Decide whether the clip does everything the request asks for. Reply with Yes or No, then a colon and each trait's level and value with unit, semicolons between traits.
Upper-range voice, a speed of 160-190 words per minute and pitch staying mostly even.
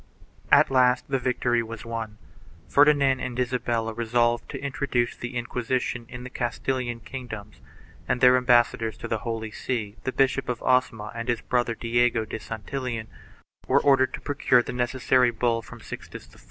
No: low, 120 Hz; average, 170 wpm; narrow, 1.8 semitones